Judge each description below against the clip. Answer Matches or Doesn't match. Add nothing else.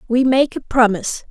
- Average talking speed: Matches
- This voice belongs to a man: Doesn't match